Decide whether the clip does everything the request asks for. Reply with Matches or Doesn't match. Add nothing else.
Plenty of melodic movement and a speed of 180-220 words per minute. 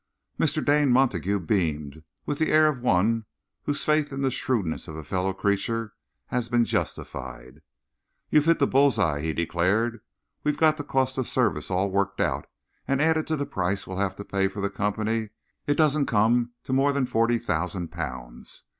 Matches